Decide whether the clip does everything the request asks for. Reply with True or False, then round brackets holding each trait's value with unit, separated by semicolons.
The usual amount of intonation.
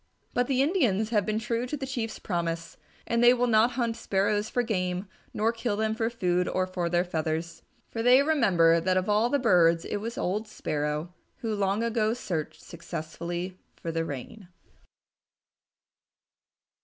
True (5.0 semitones)